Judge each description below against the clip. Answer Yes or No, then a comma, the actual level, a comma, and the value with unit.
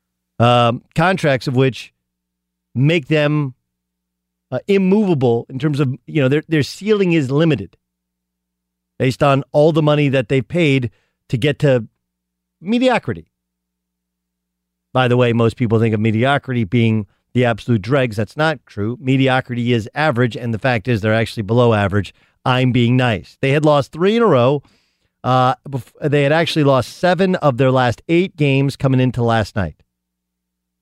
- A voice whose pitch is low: Yes, low, 125 Hz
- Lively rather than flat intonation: Yes, wide, 6.9 semitones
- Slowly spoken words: No, average, 160 wpm